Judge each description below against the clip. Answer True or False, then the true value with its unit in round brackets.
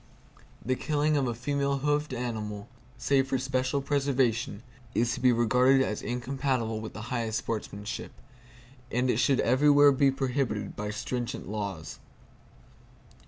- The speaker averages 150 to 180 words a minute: False (135 wpm)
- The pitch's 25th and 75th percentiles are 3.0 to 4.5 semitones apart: True (3.4 semitones)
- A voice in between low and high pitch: False (125 Hz)